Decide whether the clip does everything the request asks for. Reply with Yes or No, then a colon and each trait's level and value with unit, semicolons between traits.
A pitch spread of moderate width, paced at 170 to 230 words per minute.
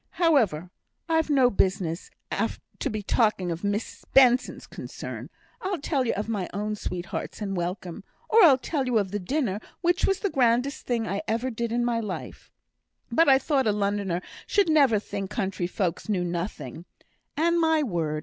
No: wide, 6.3 semitones; average, 175 wpm